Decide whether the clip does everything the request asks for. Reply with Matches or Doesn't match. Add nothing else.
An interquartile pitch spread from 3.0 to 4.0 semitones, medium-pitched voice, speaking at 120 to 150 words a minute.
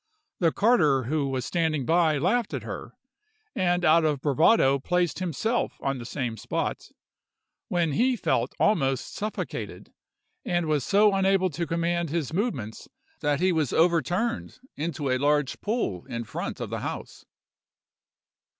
Doesn't match